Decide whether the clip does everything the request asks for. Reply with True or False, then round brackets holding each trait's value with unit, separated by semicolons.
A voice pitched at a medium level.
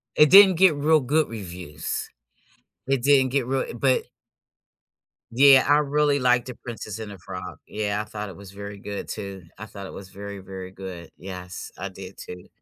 False (105 Hz)